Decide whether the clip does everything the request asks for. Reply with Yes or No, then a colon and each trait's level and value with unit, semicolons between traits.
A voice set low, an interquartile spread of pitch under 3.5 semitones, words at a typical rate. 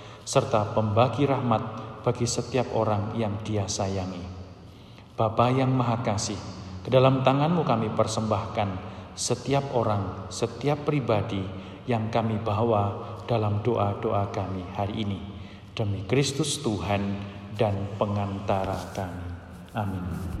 Yes: low, 105 Hz; average, 3.0 semitones; average, 110 wpm